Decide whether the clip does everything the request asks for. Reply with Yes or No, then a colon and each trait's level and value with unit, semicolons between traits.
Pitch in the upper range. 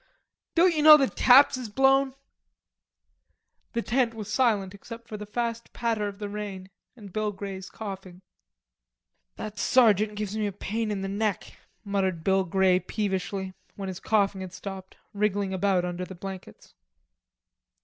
Yes: high, 205 Hz